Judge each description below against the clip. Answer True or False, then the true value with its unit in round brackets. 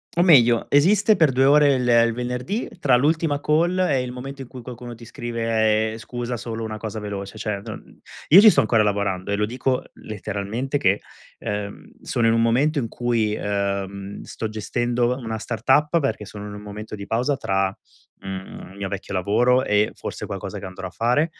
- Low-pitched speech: True (115 Hz)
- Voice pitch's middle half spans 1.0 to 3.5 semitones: False (4.2 semitones)